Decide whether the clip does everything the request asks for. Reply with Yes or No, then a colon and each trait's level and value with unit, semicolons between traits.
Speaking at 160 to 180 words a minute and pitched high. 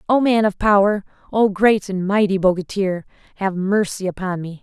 Yes: average, 170 wpm; high, 195 Hz